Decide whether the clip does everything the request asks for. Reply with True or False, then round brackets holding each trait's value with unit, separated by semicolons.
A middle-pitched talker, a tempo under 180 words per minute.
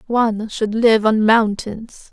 False (220 Hz; 140 wpm)